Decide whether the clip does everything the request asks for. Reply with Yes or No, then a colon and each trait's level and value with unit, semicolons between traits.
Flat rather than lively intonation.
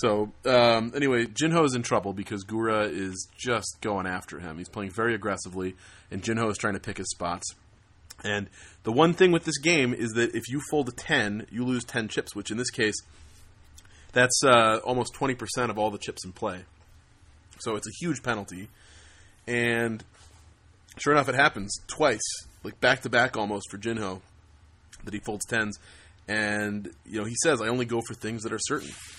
No: average, 3.9 semitones